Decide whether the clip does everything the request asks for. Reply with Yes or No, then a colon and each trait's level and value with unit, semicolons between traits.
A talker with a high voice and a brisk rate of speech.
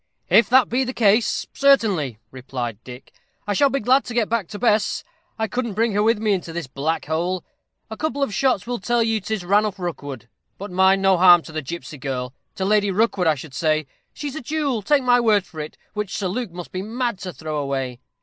Yes: high, 200 Hz; fast, 225 wpm